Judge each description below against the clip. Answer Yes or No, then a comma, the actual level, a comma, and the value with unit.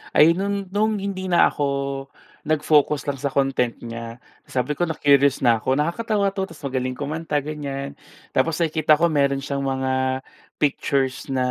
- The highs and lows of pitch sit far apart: No, average, 3.8 semitones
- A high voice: No, medium, 145 Hz